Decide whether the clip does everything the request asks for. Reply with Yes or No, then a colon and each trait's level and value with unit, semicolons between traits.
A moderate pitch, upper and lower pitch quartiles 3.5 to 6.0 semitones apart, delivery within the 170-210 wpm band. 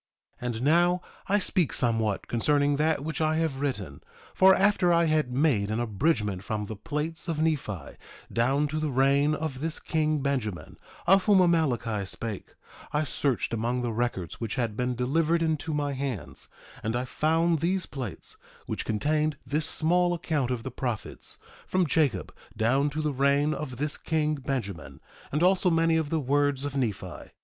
Yes: medium, 145 Hz; average, 4.7 semitones; average, 175 wpm